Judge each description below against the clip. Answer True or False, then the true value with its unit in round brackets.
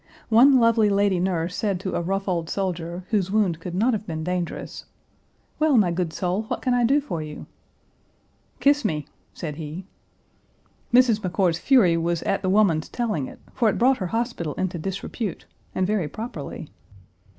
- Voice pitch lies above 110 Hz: True (190 Hz)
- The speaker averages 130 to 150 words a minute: False (175 wpm)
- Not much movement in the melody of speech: False (4.8 semitones)